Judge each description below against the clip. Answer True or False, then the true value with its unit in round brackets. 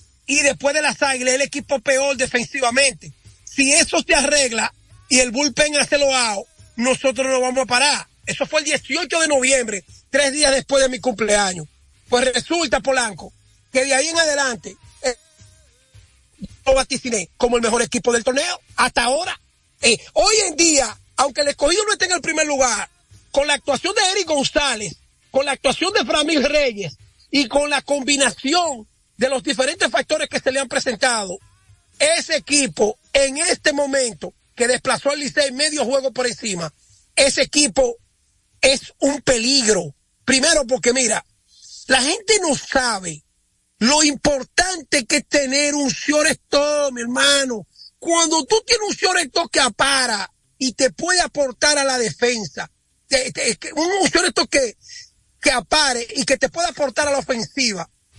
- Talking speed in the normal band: True (160 wpm)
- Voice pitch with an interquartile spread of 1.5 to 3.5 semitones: True (3.2 semitones)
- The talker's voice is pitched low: False (275 Hz)